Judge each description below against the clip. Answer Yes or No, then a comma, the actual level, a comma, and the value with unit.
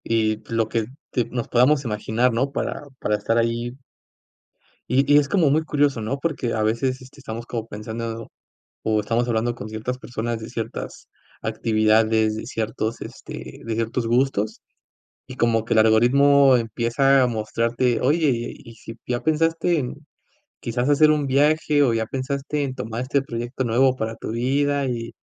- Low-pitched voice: Yes, low, 120 Hz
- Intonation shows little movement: No, average, 3.3 semitones